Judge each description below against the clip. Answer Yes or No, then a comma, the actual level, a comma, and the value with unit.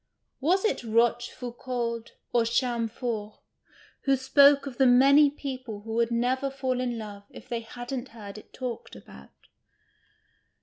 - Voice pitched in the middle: No, high, 245 Hz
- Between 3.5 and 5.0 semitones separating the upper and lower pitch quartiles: No, narrow, 2.5 semitones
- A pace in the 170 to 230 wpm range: No, slow, 135 wpm